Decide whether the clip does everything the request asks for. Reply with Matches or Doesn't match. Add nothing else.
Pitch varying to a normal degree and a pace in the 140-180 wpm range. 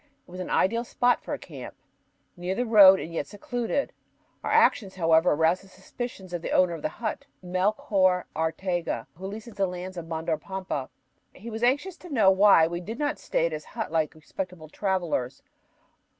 Doesn't match